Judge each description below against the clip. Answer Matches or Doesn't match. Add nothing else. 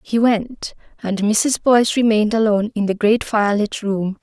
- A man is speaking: Doesn't match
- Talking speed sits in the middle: Matches